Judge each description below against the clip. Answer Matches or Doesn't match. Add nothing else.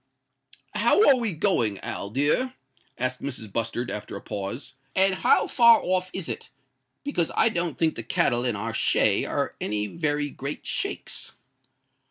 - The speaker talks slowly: Doesn't match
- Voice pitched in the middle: Matches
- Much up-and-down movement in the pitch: Matches